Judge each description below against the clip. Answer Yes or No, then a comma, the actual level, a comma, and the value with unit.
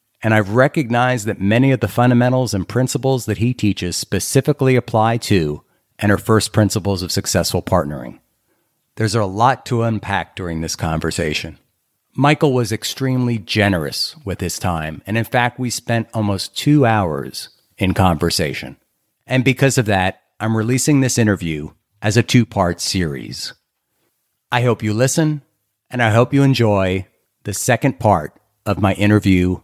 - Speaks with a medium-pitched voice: No, low, 110 Hz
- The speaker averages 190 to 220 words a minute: No, average, 155 wpm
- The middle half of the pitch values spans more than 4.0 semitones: Yes, average, 4.5 semitones